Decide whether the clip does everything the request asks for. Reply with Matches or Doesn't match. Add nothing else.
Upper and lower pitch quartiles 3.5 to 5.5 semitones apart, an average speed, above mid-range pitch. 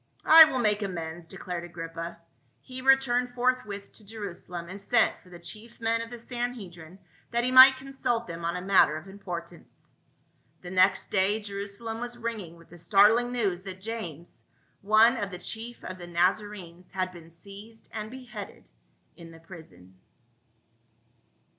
Matches